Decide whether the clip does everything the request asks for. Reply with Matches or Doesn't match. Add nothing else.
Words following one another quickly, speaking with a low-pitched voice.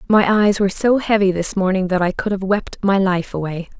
Doesn't match